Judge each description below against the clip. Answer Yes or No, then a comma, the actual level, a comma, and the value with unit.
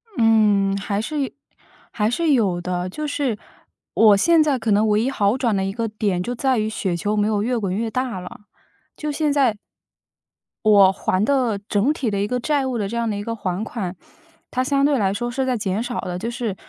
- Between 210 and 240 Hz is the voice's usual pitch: Yes, high, 220 Hz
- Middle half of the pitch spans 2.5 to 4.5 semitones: Yes, average, 4.1 semitones